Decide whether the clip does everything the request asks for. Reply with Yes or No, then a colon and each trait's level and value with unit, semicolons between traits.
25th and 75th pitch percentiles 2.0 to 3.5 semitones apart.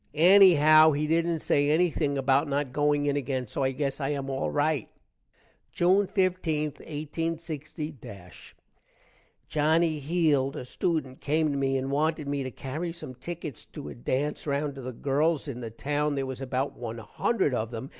Yes: average, 2.8 semitones